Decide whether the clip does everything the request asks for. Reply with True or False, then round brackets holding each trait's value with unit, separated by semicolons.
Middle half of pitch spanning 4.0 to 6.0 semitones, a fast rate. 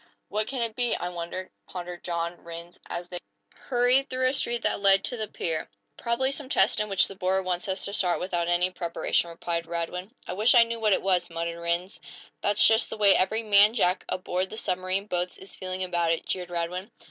False (3.5 semitones; 215 wpm)